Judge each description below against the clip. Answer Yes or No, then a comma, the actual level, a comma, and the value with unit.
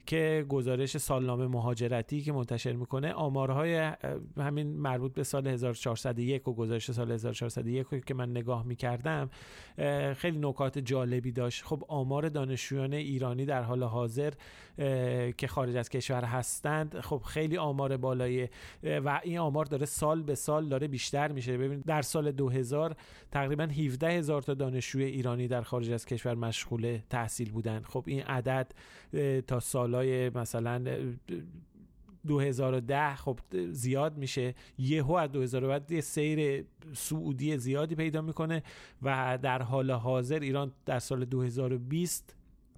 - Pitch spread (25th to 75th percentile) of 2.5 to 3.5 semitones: Yes, average, 2.9 semitones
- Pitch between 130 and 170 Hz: Yes, low, 135 Hz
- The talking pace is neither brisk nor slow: Yes, average, 135 wpm